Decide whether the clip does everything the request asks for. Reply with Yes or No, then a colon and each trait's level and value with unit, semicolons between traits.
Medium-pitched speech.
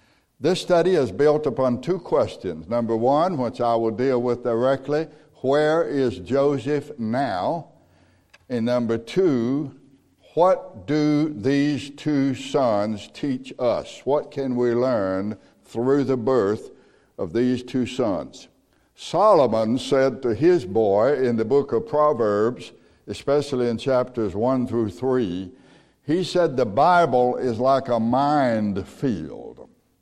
No: low, 130 Hz